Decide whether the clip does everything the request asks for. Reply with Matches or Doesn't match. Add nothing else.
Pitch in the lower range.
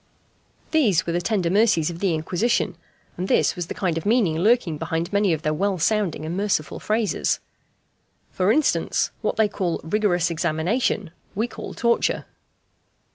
Doesn't match